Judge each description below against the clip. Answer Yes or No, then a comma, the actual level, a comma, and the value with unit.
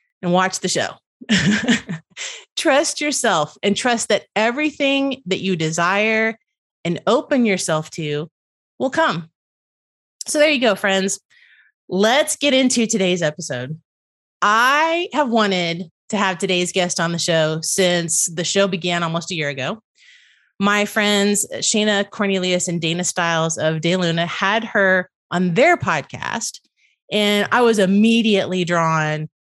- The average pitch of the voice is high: Yes, high, 195 Hz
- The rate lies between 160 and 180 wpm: No, slow, 135 wpm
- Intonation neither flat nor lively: Yes, average, 5.0 semitones